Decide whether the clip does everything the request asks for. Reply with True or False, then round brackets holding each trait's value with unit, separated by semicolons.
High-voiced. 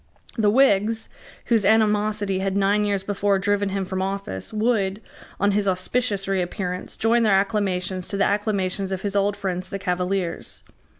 True (200 Hz)